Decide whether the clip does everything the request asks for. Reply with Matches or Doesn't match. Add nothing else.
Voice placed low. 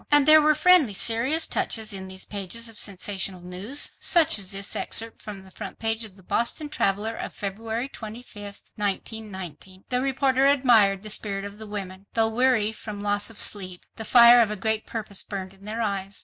Doesn't match